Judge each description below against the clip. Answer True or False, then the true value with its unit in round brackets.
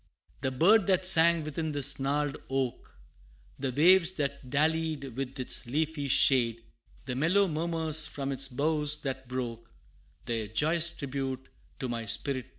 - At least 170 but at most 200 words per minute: False (150 wpm)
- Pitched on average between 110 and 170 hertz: True (140 Hz)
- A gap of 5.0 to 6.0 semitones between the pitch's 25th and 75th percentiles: False (3.6 semitones)